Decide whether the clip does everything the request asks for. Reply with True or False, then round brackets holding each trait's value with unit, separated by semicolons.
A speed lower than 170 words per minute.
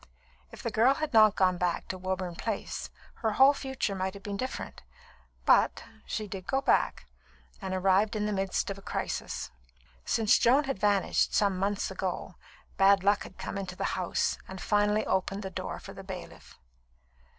False (180 wpm)